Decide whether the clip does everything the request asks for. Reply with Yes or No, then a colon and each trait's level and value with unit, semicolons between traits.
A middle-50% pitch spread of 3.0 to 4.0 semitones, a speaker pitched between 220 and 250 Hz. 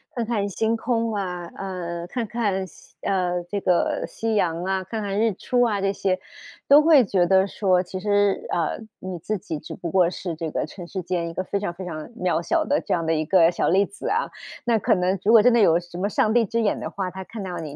No: average, 3.5 semitones; high, 190 Hz